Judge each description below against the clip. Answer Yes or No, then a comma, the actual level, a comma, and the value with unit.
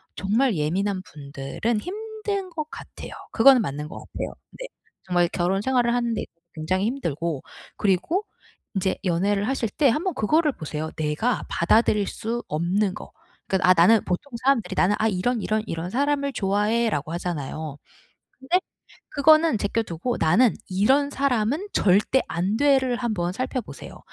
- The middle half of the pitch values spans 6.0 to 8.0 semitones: Yes, wide, 6.8 semitones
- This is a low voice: No, high, 215 Hz